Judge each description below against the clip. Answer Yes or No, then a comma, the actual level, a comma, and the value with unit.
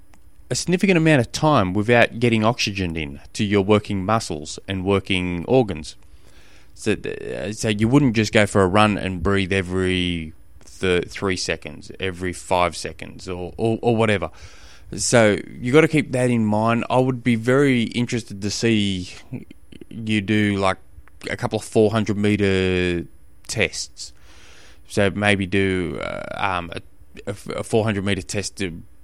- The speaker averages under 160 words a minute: Yes, average, 150 wpm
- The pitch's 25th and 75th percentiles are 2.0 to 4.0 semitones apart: Yes, average, 3.7 semitones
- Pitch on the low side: Yes, low, 100 Hz